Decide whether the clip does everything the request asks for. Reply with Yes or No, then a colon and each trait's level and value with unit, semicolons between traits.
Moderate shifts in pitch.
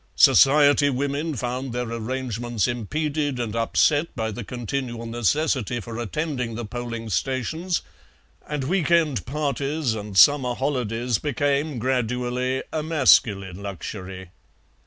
Yes: average, 3.8 semitones